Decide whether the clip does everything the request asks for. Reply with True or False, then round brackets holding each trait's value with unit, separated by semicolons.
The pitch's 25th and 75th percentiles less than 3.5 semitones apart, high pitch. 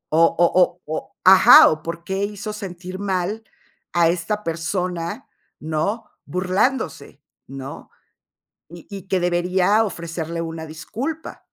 False (2.9 semitones; 180 Hz)